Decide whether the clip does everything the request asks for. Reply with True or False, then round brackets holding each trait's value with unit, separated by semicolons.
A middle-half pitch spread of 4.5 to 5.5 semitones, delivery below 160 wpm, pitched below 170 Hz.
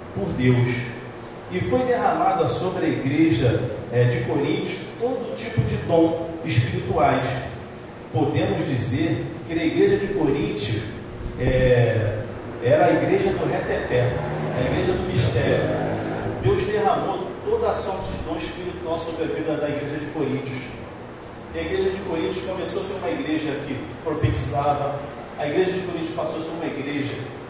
True (5.0 semitones; 150 wpm; 140 Hz)